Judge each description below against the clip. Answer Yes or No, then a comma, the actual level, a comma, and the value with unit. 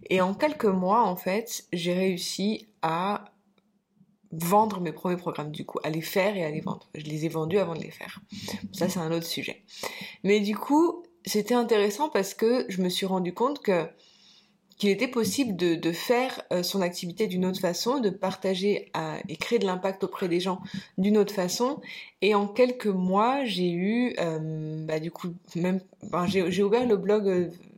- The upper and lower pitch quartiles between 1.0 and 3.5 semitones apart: Yes, average, 2.9 semitones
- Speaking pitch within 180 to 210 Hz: Yes, high, 190 Hz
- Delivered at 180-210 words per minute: Yes, average, 195 wpm